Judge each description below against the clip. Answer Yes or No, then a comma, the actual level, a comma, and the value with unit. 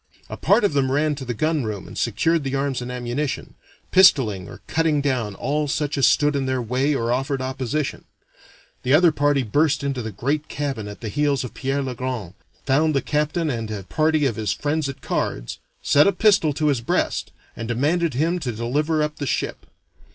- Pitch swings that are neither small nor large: Yes, average, 3.6 semitones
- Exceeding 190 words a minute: Yes, fast, 205 wpm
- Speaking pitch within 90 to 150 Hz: Yes, medium, 140 Hz